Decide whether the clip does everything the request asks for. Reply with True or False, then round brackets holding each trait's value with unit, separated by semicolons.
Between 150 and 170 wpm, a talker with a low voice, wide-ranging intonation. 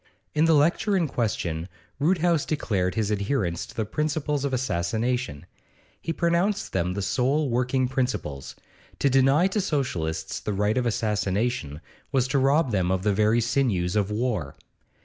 True (155 wpm; 120 Hz; 6.4 semitones)